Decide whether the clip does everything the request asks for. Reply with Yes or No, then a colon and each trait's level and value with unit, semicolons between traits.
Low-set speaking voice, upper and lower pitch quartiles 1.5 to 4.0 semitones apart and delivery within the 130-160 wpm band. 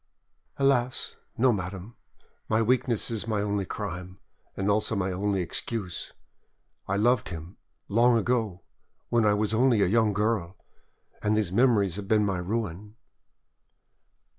Yes: low, 105 Hz; average, 3.1 semitones; average, 140 wpm